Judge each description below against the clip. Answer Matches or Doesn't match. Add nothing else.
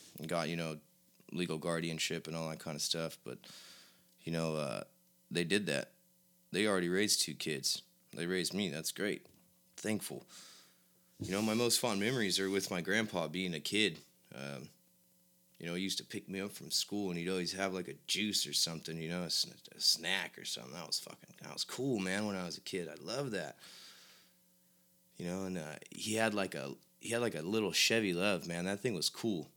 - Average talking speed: Doesn't match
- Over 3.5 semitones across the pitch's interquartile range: Matches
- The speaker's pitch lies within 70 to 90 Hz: Matches